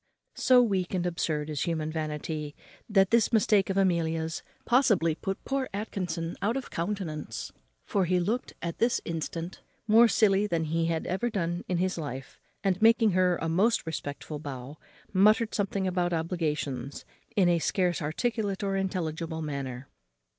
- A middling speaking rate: Yes, average, 155 wpm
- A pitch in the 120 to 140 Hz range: No, medium, 175 Hz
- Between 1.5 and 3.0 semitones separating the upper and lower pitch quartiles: No, average, 3.9 semitones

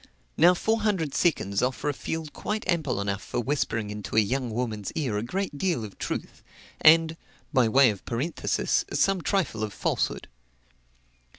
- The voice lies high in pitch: No, low, 135 Hz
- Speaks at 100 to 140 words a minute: No, average, 165 wpm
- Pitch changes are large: Yes, wide, 7.2 semitones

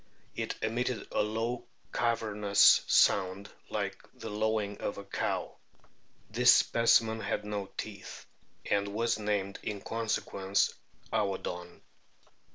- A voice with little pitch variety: Yes, narrow, 2.0 semitones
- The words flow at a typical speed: No, slow, 115 wpm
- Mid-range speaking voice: No, low, 105 Hz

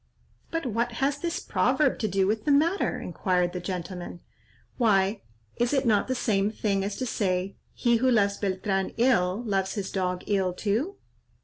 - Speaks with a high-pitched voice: Yes, high, 205 Hz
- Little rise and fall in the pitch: No, average, 4.3 semitones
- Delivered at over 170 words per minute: Yes, average, 180 wpm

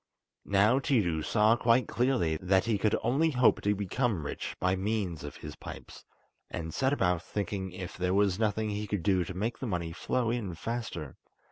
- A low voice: Yes, low, 100 Hz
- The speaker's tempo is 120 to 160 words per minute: No, average, 190 wpm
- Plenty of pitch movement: No, average, 4.4 semitones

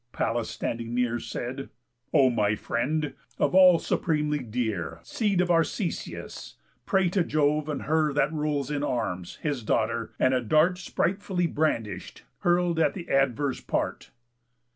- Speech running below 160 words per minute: Yes, average, 140 wpm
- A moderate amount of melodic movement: No, wide, 5.7 semitones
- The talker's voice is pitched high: No, medium, 145 Hz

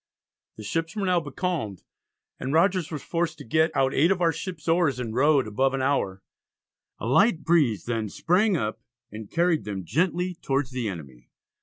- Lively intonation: Yes, wide, 7.1 semitones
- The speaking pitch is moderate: Yes, medium, 145 Hz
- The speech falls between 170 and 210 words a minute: Yes, average, 180 wpm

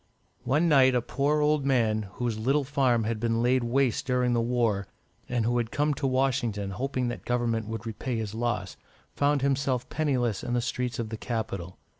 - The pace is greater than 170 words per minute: Yes, average, 190 wpm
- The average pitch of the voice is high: No, low, 120 Hz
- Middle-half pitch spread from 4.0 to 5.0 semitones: No, average, 3.0 semitones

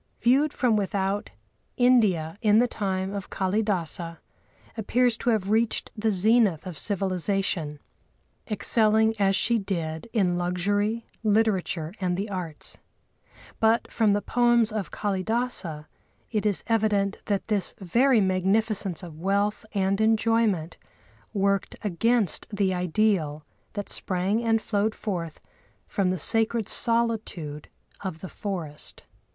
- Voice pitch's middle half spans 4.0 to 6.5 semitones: No, average, 3.2 semitones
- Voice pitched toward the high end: Yes, high, 200 Hz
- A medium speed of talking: No, slow, 125 wpm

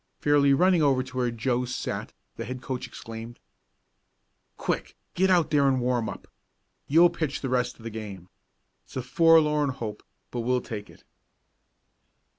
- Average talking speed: Yes, average, 160 wpm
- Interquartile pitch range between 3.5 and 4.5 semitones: Yes, average, 3.8 semitones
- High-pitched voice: No, low, 130 Hz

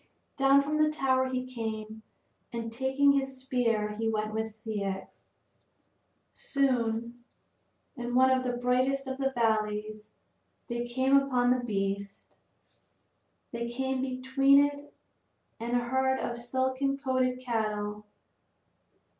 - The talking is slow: Yes, slow, 125 wpm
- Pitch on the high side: Yes, very high, 250 Hz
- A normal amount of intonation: Yes, average, 3.0 semitones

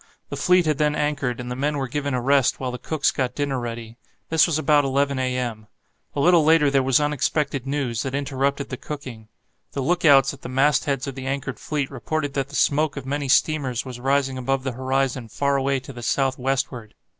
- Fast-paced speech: Yes, fast, 215 wpm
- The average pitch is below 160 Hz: Yes, low, 135 Hz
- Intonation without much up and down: Yes, narrow, 2.0 semitones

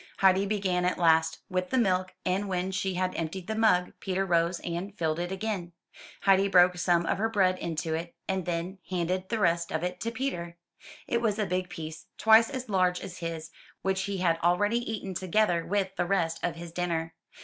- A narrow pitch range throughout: Yes, narrow, 2.3 semitones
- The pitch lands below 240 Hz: Yes, medium, 185 Hz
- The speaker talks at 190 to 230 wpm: Yes, fast, 205 wpm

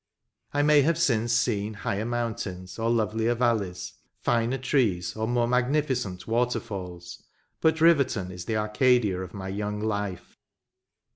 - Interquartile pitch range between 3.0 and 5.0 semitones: Yes, average, 4.0 semitones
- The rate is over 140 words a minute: No, slow, 135 wpm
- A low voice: Yes, low, 110 Hz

